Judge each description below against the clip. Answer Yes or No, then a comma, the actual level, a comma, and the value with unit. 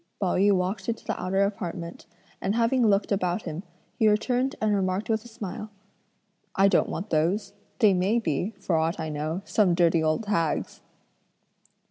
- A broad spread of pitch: No, average, 3.6 semitones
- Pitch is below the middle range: No, high, 195 Hz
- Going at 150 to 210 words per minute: Yes, average, 170 wpm